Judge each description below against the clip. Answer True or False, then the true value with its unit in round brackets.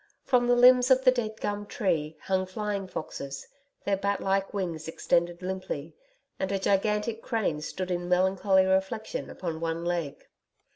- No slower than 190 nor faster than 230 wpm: False (155 wpm)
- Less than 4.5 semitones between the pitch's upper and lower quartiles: True (3.3 semitones)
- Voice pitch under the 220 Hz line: True (190 Hz)